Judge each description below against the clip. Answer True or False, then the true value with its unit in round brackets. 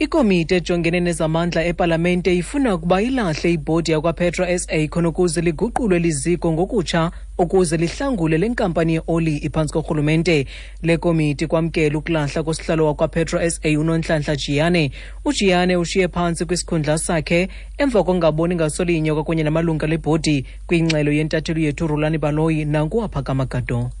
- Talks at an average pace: False (120 wpm)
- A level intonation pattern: True (2.2 semitones)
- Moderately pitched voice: True (165 Hz)